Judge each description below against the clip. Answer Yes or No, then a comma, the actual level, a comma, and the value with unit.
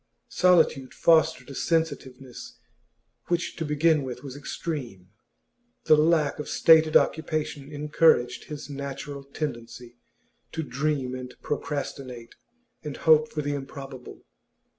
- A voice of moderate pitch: Yes, medium, 145 Hz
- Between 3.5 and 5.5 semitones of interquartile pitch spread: No, average, 3.1 semitones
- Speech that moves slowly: Yes, slow, 115 wpm